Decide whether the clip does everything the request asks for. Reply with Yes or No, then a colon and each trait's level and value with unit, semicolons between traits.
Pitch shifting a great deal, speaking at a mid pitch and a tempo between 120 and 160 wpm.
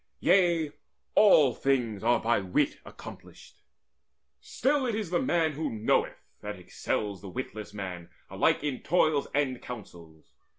No: wide, 7.6 semitones; low, 125 Hz; slow, 135 wpm